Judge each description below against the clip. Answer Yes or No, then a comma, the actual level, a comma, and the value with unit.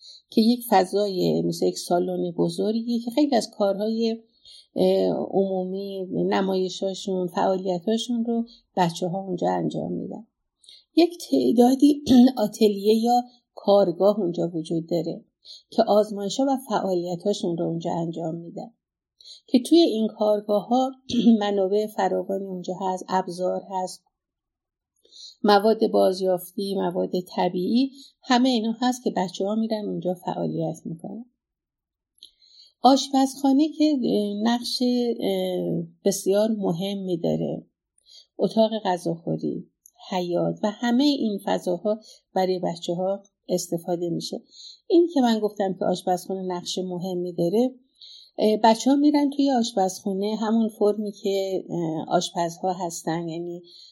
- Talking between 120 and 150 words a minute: No, average, 110 wpm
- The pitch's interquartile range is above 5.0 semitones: No, average, 4.3 semitones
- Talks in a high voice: Yes, high, 200 Hz